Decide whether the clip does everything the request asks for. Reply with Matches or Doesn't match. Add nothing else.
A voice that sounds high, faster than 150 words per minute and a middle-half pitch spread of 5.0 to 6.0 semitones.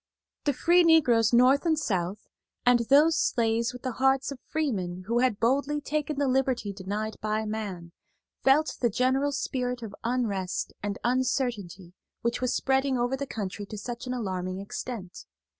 Doesn't match